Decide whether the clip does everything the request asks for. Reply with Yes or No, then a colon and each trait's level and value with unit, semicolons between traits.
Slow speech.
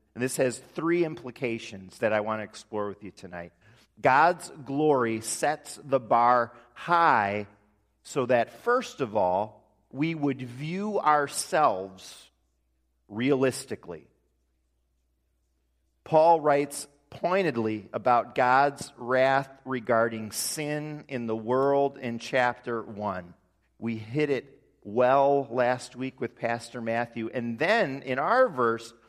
Yes: slow, 120 wpm